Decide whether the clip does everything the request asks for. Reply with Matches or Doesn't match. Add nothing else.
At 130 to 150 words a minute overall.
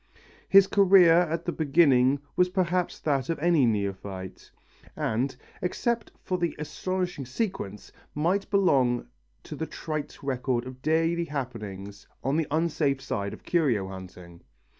Matches